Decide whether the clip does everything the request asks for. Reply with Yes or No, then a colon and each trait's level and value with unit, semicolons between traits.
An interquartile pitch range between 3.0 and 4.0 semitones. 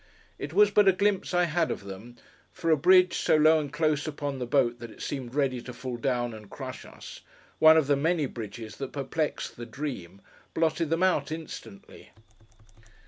No: average, 5.2 semitones